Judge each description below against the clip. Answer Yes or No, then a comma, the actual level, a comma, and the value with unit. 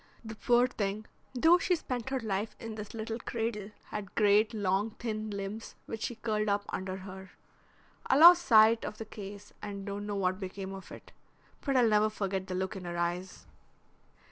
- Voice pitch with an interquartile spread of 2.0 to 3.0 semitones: Yes, narrow, 2.5 semitones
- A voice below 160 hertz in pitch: No, high, 210 Hz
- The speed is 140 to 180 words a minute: No, average, 190 wpm